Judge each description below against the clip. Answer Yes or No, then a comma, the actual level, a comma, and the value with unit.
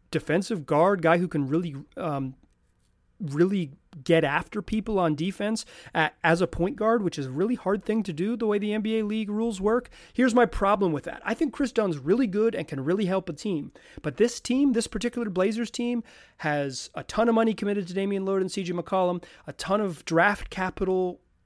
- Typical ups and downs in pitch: Yes, average, 4.6 semitones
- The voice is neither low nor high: No, high, 195 Hz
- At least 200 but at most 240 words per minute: Yes, fast, 205 wpm